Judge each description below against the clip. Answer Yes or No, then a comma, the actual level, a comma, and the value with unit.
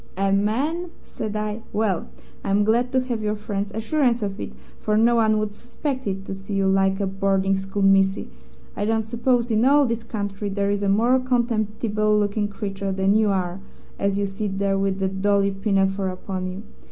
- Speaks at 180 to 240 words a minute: Yes, average, 195 wpm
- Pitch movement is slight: Yes, narrow, 2.2 semitones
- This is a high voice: Yes, high, 205 Hz